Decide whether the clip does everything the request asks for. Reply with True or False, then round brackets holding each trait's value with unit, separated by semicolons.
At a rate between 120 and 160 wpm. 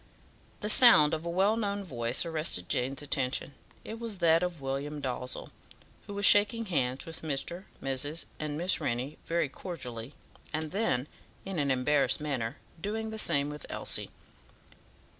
True (155 wpm)